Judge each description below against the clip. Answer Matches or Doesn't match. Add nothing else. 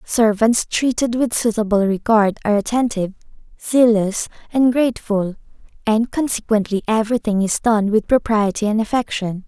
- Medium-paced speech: Doesn't match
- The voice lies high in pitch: Matches